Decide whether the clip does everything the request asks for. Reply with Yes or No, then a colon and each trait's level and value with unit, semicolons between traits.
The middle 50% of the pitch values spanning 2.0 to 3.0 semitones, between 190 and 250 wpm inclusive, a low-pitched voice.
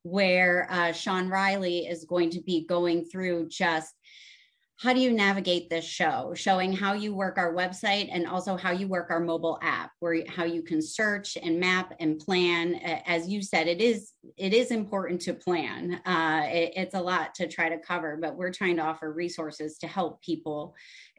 No: narrow, 2.4 semitones; average, 195 wpm; medium, 175 Hz